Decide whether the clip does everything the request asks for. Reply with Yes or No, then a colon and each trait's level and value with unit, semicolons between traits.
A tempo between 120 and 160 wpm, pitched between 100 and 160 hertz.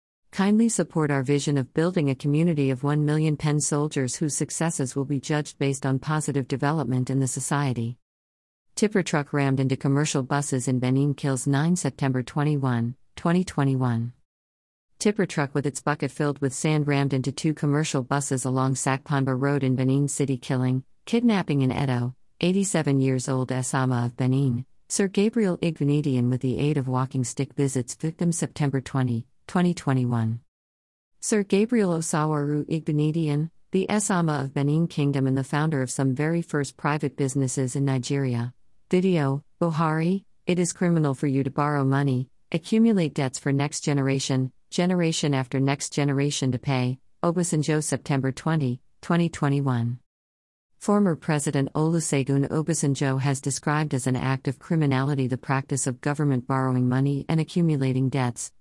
Yes: average, 150 wpm; medium, 140 Hz